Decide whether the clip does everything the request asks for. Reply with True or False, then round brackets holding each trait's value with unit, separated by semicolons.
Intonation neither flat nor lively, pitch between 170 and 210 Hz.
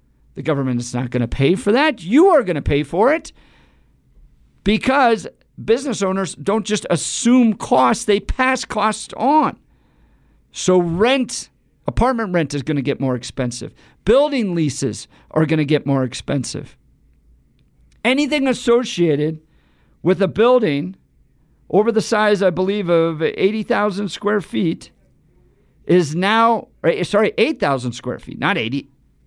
False (7.5 semitones; 190 Hz)